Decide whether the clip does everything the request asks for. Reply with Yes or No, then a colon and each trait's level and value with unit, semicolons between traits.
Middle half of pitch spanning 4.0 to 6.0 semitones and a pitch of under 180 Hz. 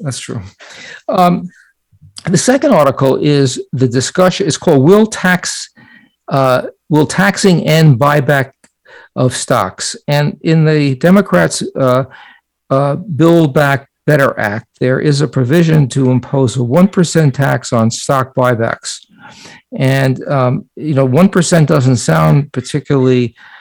Yes: average, 4.3 semitones; medium, 140 Hz